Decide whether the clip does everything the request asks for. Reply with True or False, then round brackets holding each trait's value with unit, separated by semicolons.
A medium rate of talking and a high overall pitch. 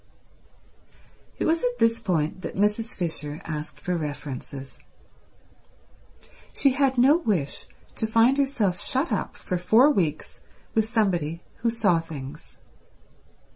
False (125 wpm; 205 Hz)